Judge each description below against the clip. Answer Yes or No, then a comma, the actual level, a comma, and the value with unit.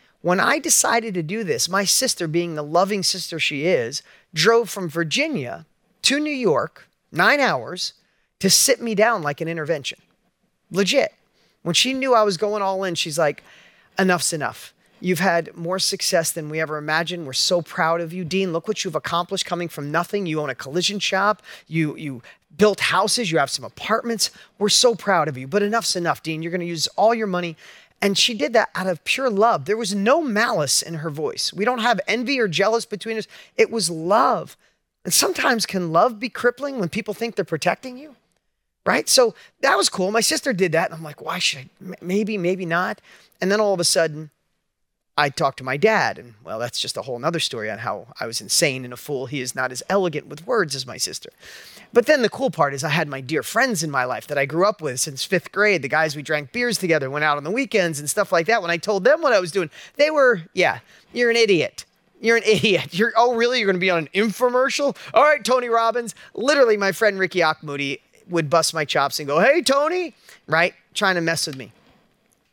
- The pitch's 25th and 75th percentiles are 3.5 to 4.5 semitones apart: No, wide, 5.6 semitones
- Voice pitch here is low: No, high, 190 Hz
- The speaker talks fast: Yes, fast, 225 wpm